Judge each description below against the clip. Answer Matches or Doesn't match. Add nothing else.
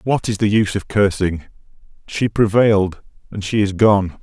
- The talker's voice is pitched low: Matches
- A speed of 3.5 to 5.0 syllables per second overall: Matches